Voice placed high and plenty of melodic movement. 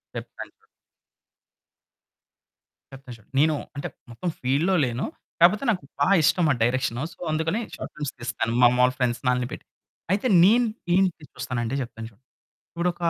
No: low, 135 Hz; wide, 6.1 semitones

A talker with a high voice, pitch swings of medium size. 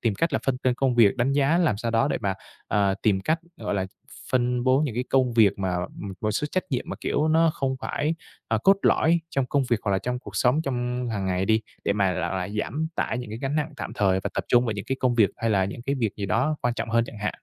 No: low, 120 Hz; average, 4.8 semitones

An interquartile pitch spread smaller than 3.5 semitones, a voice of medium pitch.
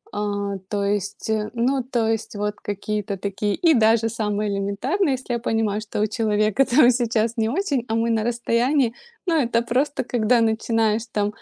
No: narrow, 2.6 semitones; high, 225 Hz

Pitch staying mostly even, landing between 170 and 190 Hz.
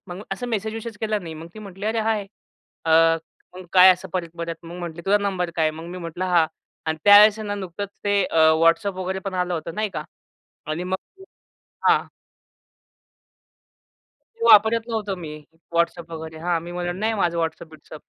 No: average, 3.5 semitones; medium, 185 Hz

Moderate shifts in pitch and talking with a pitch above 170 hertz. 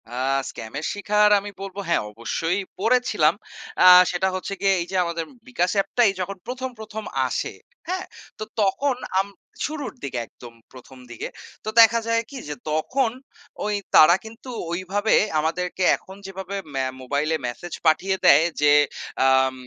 No: wide, 5.7 semitones; high, 190 Hz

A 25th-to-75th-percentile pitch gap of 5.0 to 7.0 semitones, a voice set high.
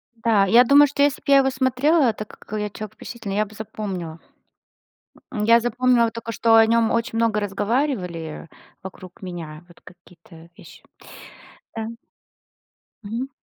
No: average, 3.7 semitones; high, 220 Hz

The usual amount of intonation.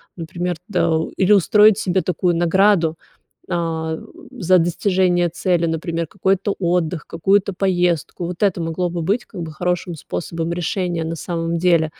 No: narrow, 2.0 semitones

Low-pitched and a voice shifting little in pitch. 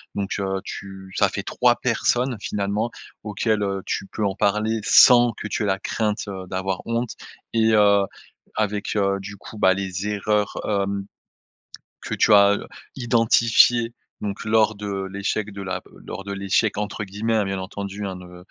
Yes: low, 100 Hz; narrow, 1.8 semitones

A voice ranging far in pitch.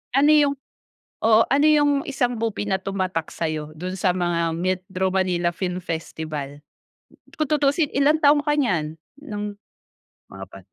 Yes: wide, 8.8 semitones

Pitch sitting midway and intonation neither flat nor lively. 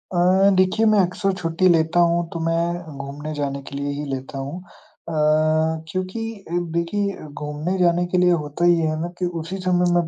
Yes: medium, 170 Hz; average, 3.1 semitones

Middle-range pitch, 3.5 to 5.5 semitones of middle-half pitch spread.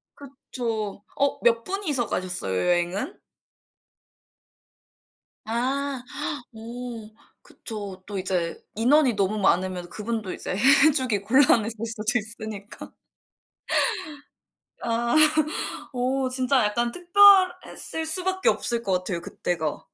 No: high, 230 Hz; average, 5.1 semitones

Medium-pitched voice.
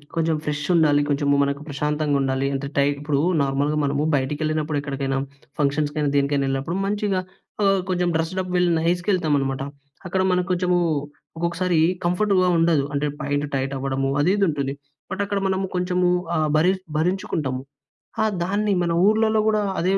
Yes: medium, 155 Hz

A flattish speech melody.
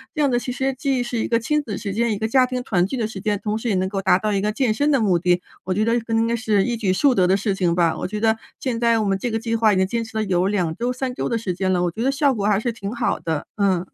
No: average, 3.7 semitones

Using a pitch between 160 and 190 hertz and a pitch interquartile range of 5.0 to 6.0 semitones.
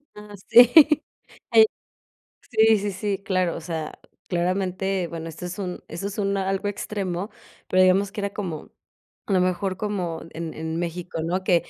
No: medium, 185 Hz; average, 2.7 semitones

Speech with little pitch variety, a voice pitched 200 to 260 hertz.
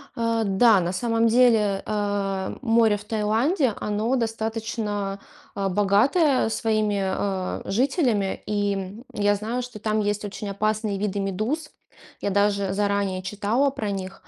Yes: narrow, 2.3 semitones; high, 210 Hz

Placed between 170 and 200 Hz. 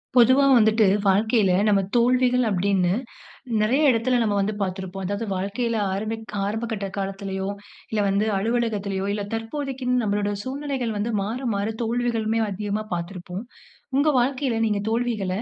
No: high, 215 Hz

